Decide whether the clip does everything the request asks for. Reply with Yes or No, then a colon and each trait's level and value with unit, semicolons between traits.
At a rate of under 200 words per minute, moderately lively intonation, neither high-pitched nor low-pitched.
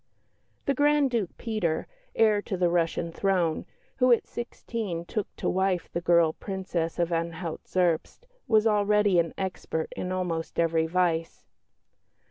Yes: average, 140 wpm; average, 3.9 semitones; medium, 180 Hz